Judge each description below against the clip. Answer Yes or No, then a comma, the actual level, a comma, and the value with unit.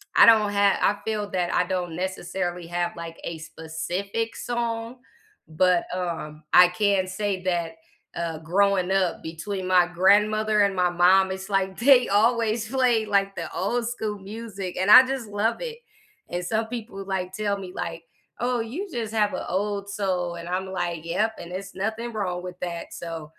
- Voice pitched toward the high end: Yes, high, 195 Hz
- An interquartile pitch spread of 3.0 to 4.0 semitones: Yes, average, 3.3 semitones